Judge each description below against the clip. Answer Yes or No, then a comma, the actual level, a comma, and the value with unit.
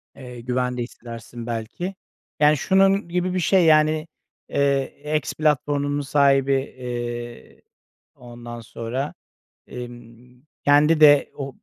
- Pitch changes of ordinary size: Yes, average, 4.0 semitones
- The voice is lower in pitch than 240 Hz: Yes, low, 135 Hz